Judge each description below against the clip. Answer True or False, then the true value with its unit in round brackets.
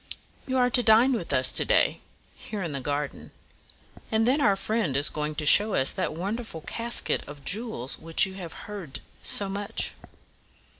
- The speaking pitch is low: False (195 Hz)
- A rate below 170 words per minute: False (185 wpm)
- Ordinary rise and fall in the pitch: False (6.9 semitones)